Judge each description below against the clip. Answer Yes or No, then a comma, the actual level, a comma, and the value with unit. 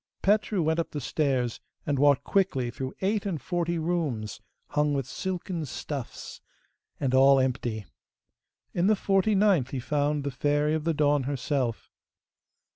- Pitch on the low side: No, medium, 145 Hz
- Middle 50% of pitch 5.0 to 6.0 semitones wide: No, average, 4.6 semitones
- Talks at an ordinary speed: Yes, average, 150 wpm